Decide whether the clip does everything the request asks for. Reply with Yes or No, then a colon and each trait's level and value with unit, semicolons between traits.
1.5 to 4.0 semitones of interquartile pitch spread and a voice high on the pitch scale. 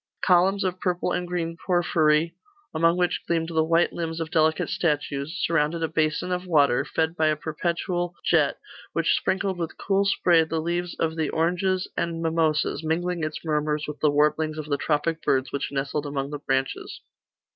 No: narrow, 2.4 semitones; medium, 160 Hz